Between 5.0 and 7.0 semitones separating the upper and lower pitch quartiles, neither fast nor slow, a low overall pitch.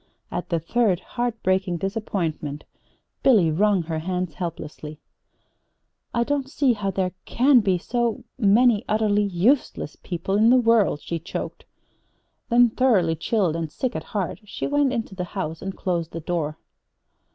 No: wide, 5.6 semitones; average, 150 wpm; high, 195 Hz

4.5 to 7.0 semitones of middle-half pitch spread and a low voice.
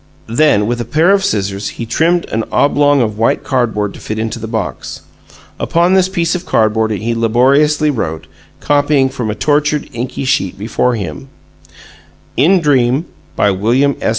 Yes: wide, 5.4 semitones; low, 125 Hz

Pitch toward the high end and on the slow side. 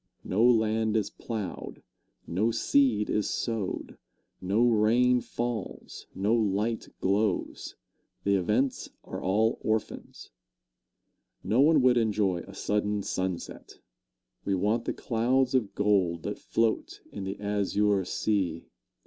No: low, 105 Hz; slow, 120 wpm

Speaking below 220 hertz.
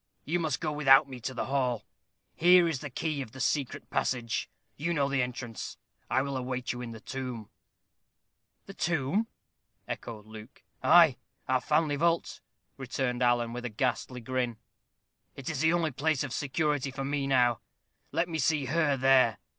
Yes: low, 135 Hz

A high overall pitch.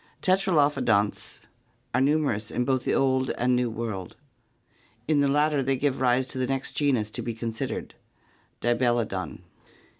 No: low, 130 Hz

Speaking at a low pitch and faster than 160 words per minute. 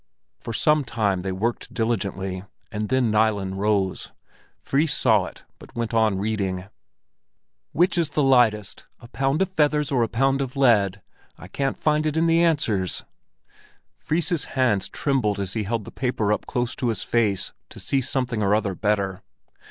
Yes: low, 115 Hz; average, 170 wpm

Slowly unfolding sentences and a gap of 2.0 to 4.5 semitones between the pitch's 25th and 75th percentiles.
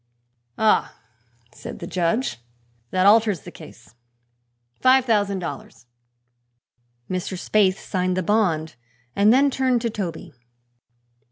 Yes: slow, 110 wpm; average, 3.8 semitones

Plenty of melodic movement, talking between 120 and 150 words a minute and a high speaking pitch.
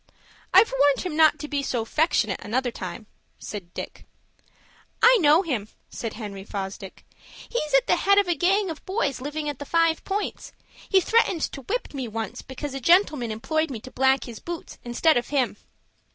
No: wide, 6.1 semitones; average, 185 wpm; very high, 285 Hz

